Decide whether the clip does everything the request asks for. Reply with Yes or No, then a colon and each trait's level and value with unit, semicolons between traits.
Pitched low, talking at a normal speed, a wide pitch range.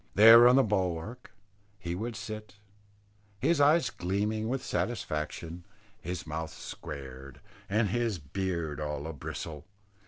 No: very low, 95 Hz; slow, 125 wpm; wide, 5.8 semitones